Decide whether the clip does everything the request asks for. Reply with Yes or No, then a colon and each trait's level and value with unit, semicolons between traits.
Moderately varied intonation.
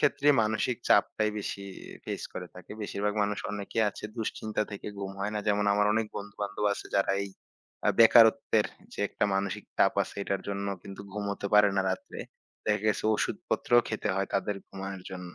No: narrow, 1.5 semitones